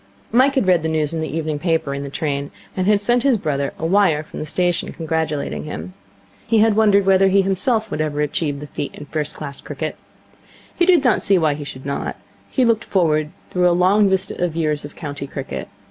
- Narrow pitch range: No, average, 5.0 semitones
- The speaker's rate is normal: No, fast, 225 wpm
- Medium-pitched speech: Yes, medium, 165 Hz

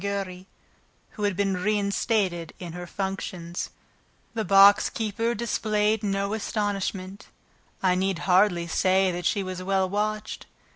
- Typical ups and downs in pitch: No, narrow, 2.1 semitones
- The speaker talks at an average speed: No, slow, 130 wpm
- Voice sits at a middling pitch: No, high, 195 Hz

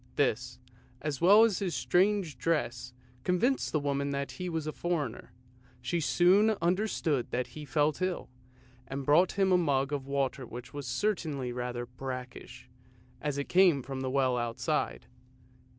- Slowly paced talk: No, average, 155 wpm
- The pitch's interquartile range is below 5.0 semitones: No, average, 5.3 semitones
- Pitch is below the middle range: No, medium, 145 Hz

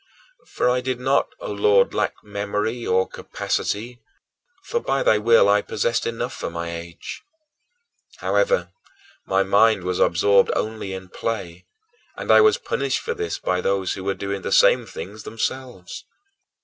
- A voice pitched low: Yes, low, 105 Hz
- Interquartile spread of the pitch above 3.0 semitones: Yes, average, 4.0 semitones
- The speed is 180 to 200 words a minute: No, average, 155 wpm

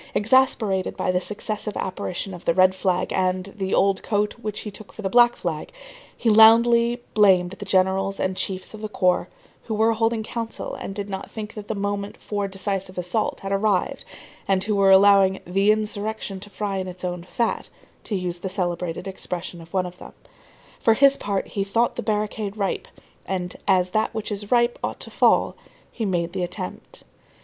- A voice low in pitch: No, high, 195 Hz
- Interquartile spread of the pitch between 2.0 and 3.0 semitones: Yes, narrow, 2.5 semitones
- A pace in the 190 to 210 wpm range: Yes, average, 195 wpm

